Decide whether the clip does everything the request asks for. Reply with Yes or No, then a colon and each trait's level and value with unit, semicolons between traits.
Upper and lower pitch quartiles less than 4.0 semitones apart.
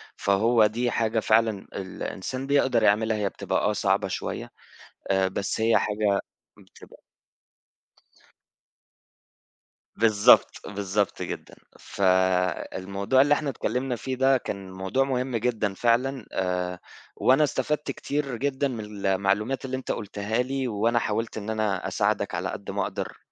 No: average, 4.5 semitones